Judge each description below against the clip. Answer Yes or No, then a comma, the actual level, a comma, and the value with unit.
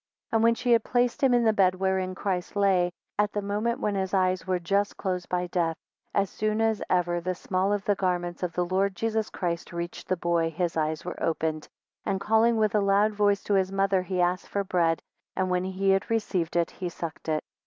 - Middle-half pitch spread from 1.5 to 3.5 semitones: Yes, narrow, 2.6 semitones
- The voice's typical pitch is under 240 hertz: Yes, high, 190 Hz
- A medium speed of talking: No, fast, 230 wpm